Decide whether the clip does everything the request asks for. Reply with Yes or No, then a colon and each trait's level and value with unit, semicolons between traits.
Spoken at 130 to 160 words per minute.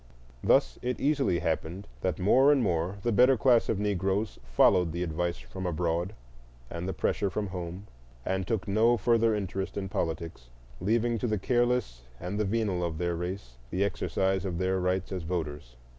No: average, 175 wpm